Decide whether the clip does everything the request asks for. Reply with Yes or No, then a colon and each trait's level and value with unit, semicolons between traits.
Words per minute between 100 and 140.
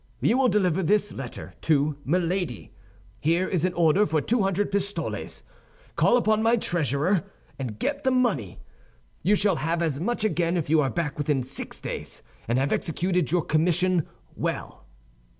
No: average, 165 wpm